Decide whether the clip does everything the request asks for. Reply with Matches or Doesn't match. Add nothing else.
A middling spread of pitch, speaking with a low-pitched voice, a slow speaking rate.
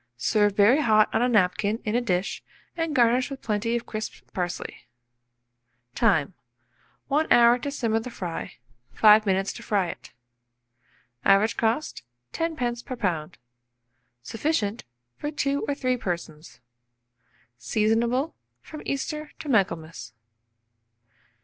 Doesn't match